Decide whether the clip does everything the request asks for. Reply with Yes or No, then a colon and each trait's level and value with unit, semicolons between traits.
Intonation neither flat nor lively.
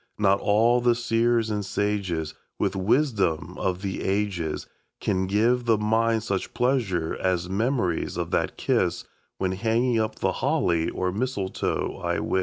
Yes: average, 3.7 semitones